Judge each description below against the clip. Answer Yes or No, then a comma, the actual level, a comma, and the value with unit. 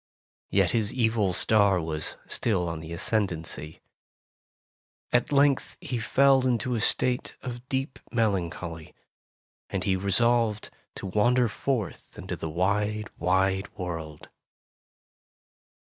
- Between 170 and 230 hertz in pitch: No, low, 105 Hz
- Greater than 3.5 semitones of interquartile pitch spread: Yes, average, 5.1 semitones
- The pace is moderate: No, slow, 115 wpm